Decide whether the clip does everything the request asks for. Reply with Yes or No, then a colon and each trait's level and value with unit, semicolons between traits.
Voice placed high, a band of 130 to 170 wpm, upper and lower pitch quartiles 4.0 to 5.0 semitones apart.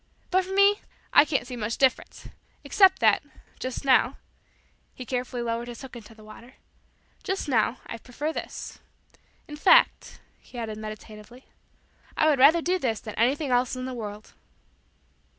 Yes: very high, 250 Hz; average, 165 wpm; average, 4.4 semitones